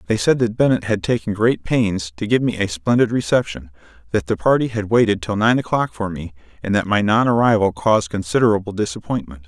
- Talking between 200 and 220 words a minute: Yes, fast, 205 wpm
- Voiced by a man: Yes, male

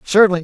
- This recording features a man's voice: Yes, male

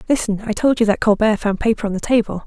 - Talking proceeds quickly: Yes, fast, 270 wpm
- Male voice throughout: No, female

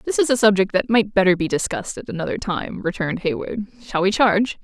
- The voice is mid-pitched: No, high, 200 Hz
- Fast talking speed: Yes, fast, 220 wpm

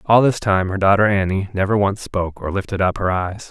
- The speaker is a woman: No, male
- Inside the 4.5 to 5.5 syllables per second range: No, 5.7 syllables/s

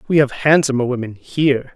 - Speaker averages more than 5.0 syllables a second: Yes, 5.7 syllables/s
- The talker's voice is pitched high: No, low, 135 Hz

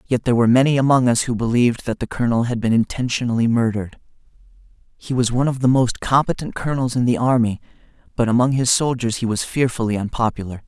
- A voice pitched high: No, low, 120 Hz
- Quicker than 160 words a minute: Yes, average, 190 wpm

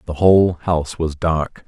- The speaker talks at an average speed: Yes, average, 180 wpm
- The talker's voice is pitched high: No, very low, 85 Hz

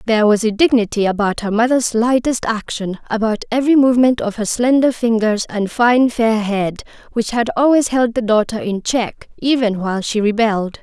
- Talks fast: No, average, 175 wpm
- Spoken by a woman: Yes, female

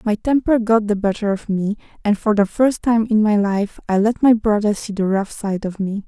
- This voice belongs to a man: No, female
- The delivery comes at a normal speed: No, fast, 245 wpm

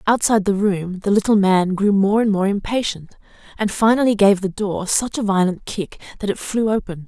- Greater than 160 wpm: Yes, fast, 205 wpm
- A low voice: No, high, 200 Hz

